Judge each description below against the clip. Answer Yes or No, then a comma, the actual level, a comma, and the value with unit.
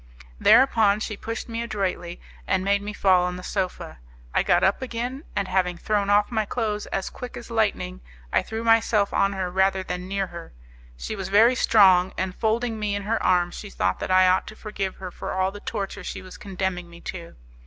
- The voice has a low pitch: No, high, 200 Hz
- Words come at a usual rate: No, fast, 210 wpm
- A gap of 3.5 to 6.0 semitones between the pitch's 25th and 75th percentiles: No, average, 2.7 semitones